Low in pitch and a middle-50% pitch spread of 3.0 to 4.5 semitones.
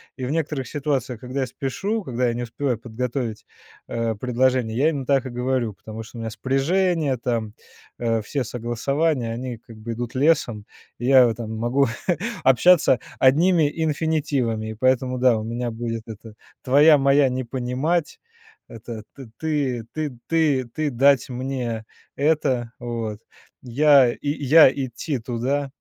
Yes: low, 130 Hz; average, 3.4 semitones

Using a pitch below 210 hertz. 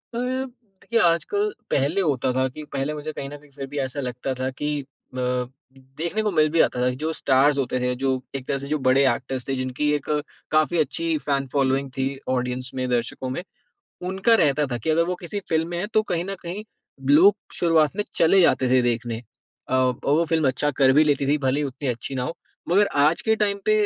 Yes: medium, 140 Hz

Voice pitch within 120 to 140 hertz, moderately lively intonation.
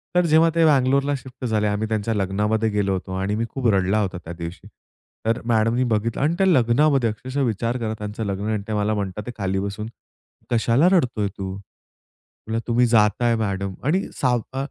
No: low, 110 Hz; average, 3.5 semitones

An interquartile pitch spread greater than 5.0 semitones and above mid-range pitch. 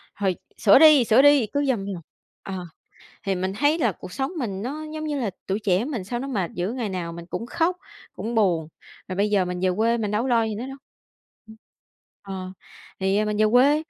Yes: wide, 5.5 semitones; high, 215 Hz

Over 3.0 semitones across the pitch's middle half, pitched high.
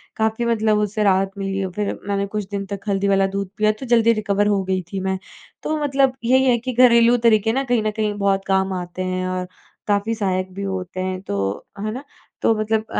No: average, 2.7 semitones; high, 205 Hz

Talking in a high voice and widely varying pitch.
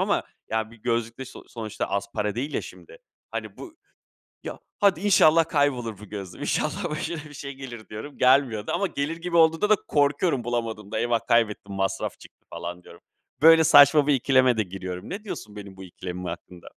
No: low, 120 Hz; wide, 6.4 semitones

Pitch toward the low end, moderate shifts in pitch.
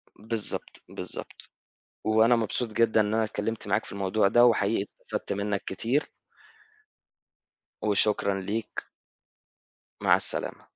No: low, 110 Hz; narrow, 1.9 semitones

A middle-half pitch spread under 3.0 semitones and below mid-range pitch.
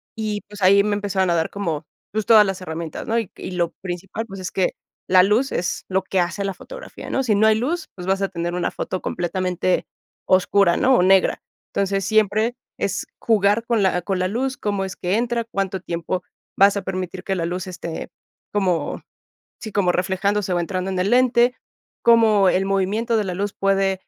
No: narrow, 2.5 semitones; high, 195 Hz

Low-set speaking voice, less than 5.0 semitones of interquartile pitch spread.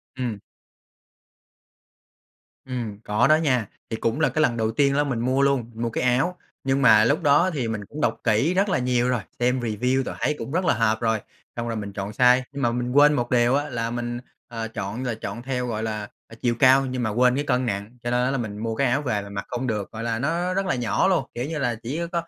Yes: low, 125 Hz; average, 3.4 semitones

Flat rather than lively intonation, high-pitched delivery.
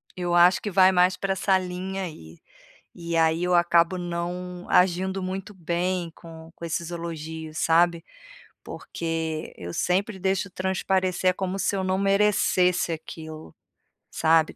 No: narrow, 2.2 semitones; medium, 180 Hz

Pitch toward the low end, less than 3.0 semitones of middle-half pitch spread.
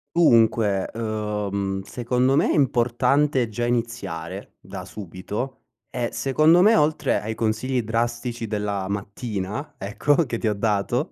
No: low, 115 Hz; average, 3.7 semitones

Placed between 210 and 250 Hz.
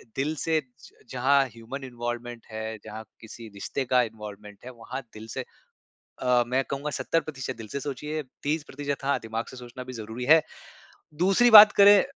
No: low, 125 Hz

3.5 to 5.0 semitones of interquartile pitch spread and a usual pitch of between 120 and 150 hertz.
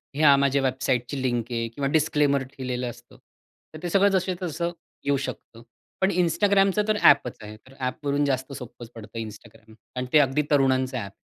Yes: average, 4.0 semitones; low, 135 Hz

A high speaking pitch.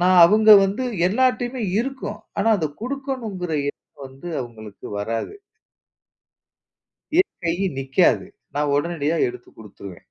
No: medium, 175 Hz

